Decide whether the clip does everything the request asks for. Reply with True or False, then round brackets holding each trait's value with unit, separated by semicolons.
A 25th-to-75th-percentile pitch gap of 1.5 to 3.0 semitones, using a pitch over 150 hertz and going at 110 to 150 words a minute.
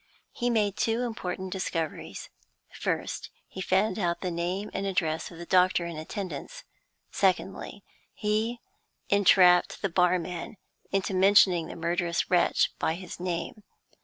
True (2.6 semitones; 185 Hz; 135 wpm)